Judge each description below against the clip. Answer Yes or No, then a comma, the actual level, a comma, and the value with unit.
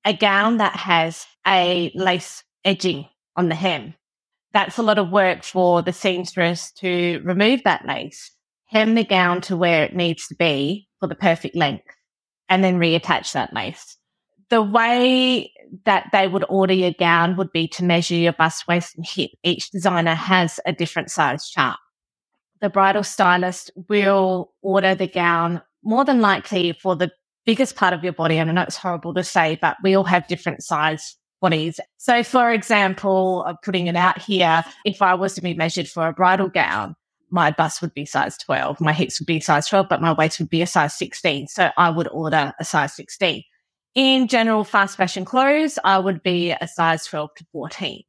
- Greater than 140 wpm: Yes, average, 190 wpm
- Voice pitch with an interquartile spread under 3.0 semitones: Yes, narrow, 2.6 semitones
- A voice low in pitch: No, medium, 180 Hz